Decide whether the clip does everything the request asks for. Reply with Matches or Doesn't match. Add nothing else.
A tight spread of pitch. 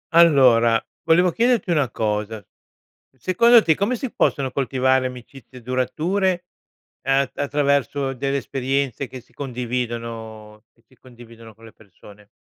Doesn't match